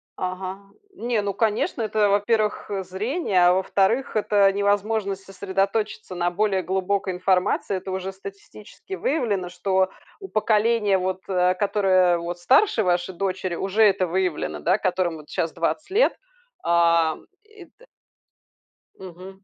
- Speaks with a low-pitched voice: No, high, 195 Hz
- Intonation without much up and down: Yes, narrow, 2.3 semitones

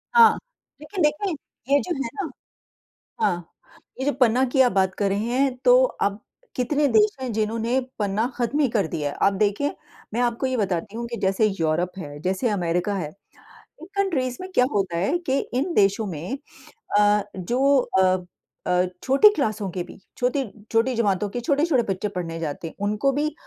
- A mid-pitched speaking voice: No, high, 225 Hz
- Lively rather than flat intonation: Yes, wide, 5.9 semitones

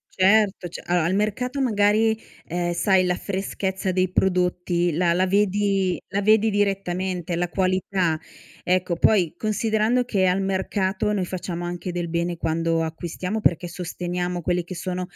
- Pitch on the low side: No, medium, 185 Hz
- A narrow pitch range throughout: Yes, narrow, 2.3 semitones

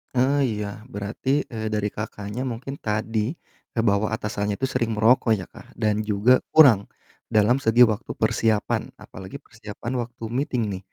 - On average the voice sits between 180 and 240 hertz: No, low, 110 Hz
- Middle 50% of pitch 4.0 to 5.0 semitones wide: No, average, 2.8 semitones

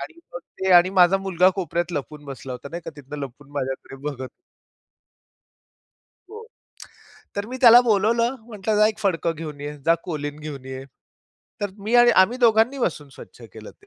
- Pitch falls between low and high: Yes, medium, 175 Hz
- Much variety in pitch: Yes, wide, 6.9 semitones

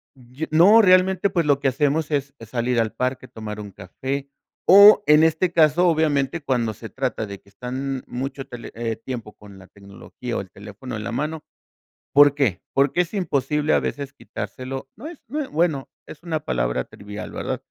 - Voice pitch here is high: No, low, 135 Hz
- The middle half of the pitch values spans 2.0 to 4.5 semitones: No, average, 5.2 semitones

